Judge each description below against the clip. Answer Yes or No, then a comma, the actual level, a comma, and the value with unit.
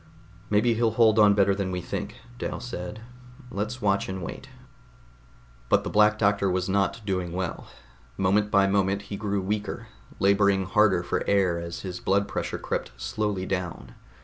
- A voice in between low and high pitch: No, low, 100 Hz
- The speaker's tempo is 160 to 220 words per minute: Yes, average, 165 wpm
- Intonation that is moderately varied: No, narrow, 2.0 semitones